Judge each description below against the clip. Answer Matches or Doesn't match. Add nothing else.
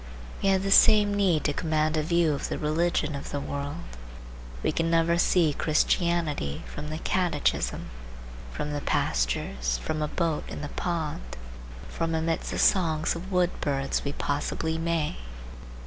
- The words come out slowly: Doesn't match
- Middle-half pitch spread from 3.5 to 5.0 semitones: Doesn't match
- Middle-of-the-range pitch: Matches